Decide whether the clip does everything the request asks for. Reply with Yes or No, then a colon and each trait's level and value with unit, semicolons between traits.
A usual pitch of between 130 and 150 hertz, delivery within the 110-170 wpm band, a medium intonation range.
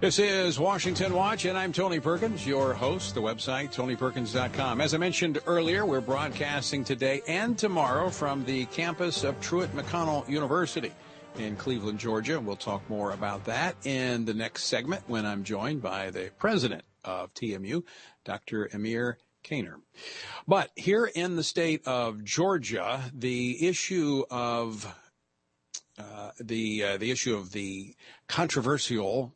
No: low, 135 Hz; average, 145 wpm; wide, 7.1 semitones